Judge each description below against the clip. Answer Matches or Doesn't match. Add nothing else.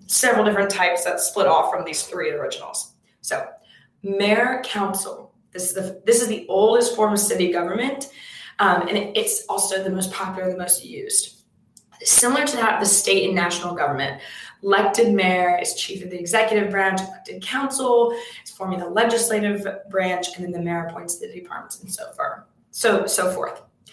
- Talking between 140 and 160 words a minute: Doesn't match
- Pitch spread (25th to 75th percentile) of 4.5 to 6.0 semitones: Matches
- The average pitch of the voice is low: Doesn't match